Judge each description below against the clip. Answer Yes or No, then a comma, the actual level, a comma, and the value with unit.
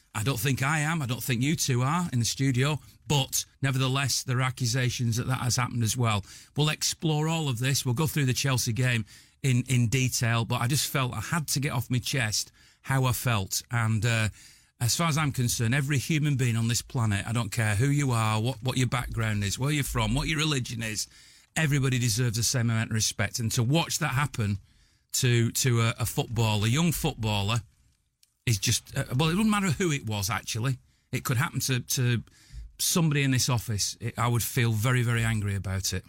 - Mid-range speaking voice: No, low, 125 Hz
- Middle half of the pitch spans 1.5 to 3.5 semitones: Yes, average, 3.2 semitones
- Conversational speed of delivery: No, fast, 220 wpm